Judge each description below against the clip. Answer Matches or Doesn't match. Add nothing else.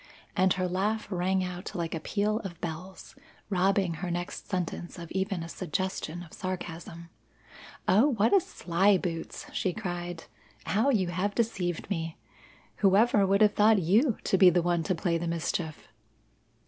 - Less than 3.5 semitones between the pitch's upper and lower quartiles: Matches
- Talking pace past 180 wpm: Doesn't match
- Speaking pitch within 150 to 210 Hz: Matches